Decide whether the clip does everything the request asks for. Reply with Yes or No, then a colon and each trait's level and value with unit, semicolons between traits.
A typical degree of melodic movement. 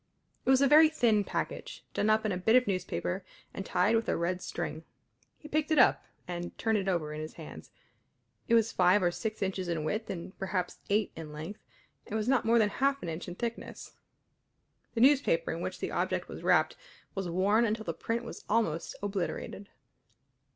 Yes: average, 4.4 semitones